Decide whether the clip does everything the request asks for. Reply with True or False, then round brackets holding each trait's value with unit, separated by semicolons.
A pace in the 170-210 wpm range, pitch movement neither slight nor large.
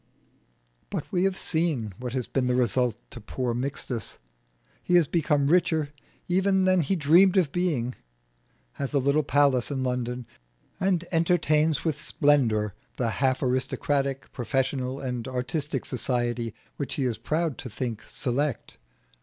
False (145 wpm; 4.1 semitones)